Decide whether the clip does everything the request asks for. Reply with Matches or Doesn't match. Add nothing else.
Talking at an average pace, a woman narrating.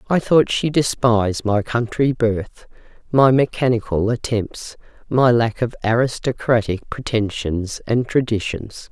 Doesn't match